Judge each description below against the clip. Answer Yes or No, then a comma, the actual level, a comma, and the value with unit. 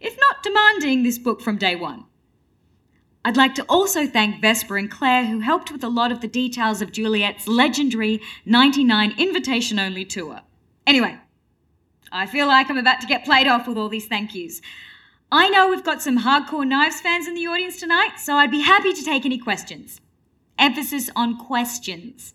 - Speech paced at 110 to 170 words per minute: No, average, 185 wpm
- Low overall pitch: No, very high, 255 Hz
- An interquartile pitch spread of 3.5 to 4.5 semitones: No, average, 4.9 semitones